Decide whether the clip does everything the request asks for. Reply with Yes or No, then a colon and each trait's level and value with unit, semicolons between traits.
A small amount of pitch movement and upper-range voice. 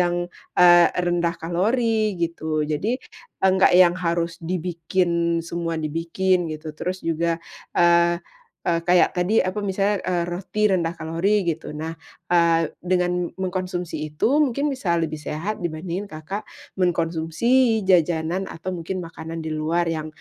No: narrow, 2.1 semitones; medium, 175 Hz